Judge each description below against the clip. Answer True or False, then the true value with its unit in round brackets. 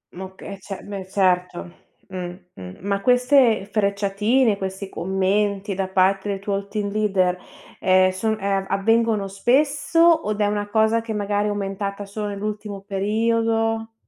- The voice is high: True (200 Hz)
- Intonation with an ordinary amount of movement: False (2.1 semitones)